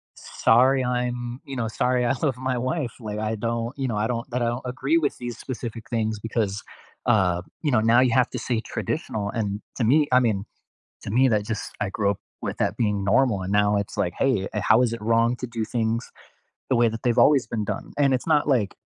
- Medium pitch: No, low, 115 Hz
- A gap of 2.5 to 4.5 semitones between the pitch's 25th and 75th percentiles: Yes, average, 2.8 semitones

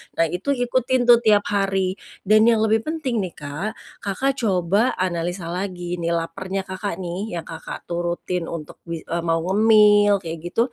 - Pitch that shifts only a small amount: No, average, 3.9 semitones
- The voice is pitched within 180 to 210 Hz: Yes, high, 190 Hz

